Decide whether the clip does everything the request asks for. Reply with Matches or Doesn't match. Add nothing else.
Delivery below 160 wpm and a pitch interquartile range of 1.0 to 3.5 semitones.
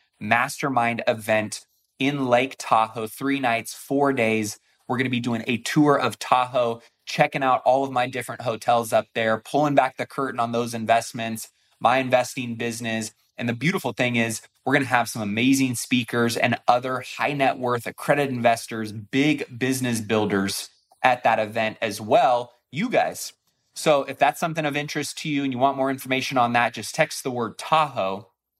Doesn't match